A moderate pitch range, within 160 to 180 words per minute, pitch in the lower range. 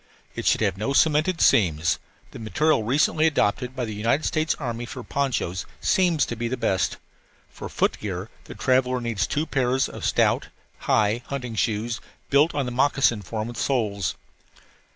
Yes: average, 4.5 semitones; average, 165 wpm; low, 120 Hz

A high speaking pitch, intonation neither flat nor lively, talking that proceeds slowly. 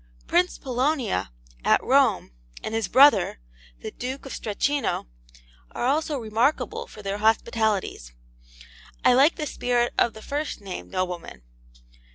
Yes: high, 240 Hz; average, 5.0 semitones; slow, 130 wpm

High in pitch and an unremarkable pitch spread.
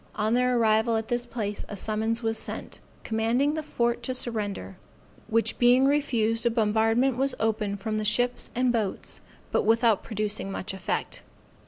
No: high, 225 Hz; narrow, 2.2 semitones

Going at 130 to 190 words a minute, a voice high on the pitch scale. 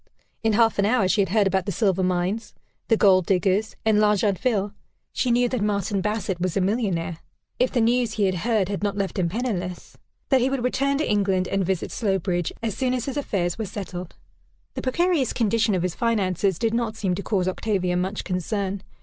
No: fast, 205 wpm; high, 205 Hz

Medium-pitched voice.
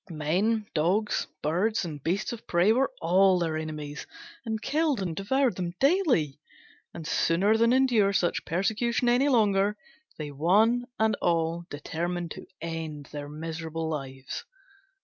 Yes: medium, 180 Hz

